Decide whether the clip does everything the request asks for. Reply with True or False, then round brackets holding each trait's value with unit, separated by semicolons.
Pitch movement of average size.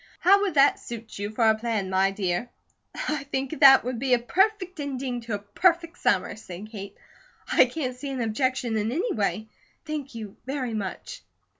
True (4.9 semitones)